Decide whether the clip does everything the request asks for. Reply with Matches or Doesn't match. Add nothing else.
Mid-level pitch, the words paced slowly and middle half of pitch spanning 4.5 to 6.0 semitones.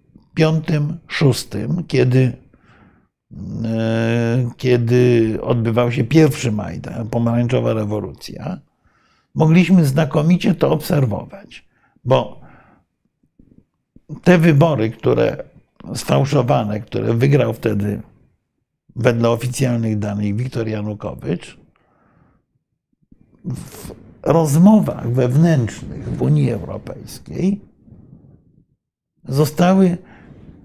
Doesn't match